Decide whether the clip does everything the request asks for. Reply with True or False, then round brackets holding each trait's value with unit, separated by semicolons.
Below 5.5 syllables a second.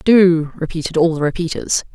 True (5.2 syllables/s)